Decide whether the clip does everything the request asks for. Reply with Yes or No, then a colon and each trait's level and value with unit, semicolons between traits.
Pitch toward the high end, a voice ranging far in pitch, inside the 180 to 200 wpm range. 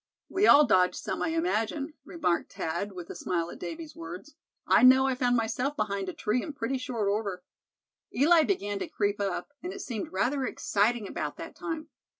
Yes: high, 235 Hz; wide, 6.5 semitones; average, 190 wpm